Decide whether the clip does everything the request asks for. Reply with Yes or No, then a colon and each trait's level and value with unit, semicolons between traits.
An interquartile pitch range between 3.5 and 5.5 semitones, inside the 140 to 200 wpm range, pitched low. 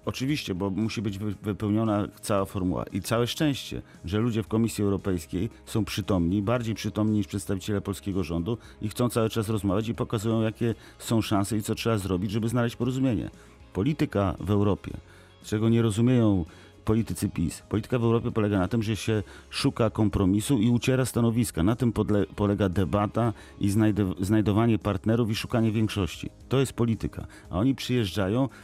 No: narrow, 2.6 semitones; fast, 160 wpm; low, 105 Hz